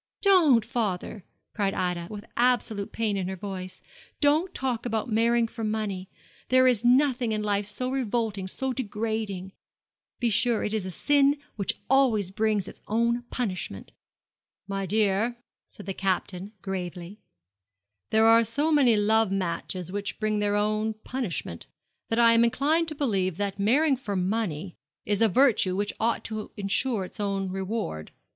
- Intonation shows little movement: No, average, 3.5 semitones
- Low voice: No, high, 215 Hz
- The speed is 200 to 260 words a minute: No, average, 155 wpm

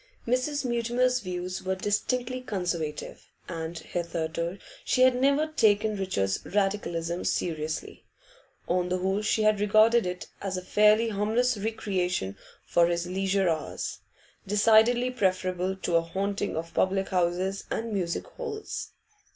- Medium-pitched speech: No, high, 195 Hz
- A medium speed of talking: No, slow, 130 wpm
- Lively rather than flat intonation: No, average, 4.1 semitones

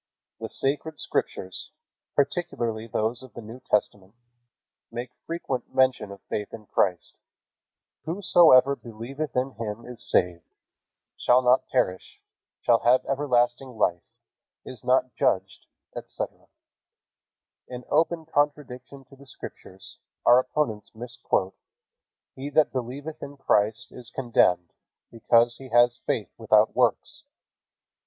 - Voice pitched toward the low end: Yes, low, 125 Hz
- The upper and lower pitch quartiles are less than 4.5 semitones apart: Yes, average, 3.5 semitones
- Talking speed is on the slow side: Yes, slow, 120 wpm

